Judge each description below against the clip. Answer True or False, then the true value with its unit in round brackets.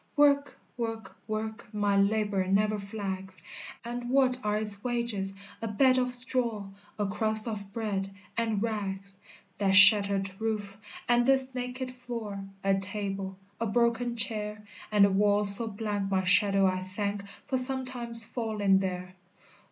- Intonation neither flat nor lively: True (3.1 semitones)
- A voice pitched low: False (210 Hz)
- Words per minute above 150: False (145 wpm)